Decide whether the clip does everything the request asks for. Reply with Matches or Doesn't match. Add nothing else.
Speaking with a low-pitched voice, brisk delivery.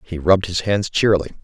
Matches